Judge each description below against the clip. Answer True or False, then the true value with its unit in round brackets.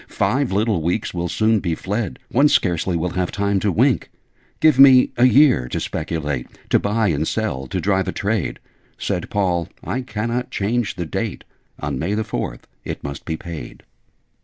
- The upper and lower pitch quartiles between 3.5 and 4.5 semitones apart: False (5.0 semitones)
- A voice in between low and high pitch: False (100 Hz)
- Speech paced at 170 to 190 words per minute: True (185 wpm)